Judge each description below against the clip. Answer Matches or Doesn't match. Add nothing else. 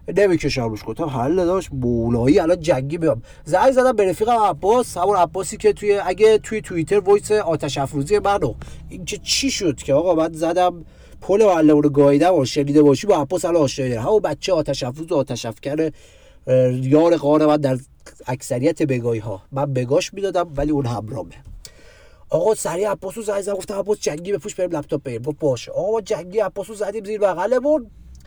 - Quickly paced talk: Matches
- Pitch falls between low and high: Matches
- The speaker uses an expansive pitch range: Matches